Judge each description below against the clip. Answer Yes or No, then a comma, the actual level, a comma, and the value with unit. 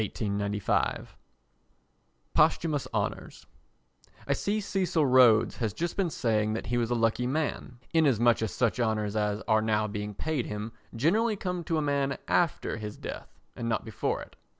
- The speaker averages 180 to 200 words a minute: No, average, 160 wpm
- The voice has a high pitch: No, low, 120 Hz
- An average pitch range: No, wide, 6.5 semitones